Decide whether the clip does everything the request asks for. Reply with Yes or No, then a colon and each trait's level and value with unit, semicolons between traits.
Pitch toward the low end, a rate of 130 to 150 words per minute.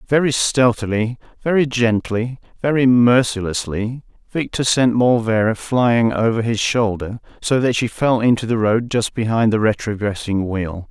Yes: low, 115 Hz; average, 140 wpm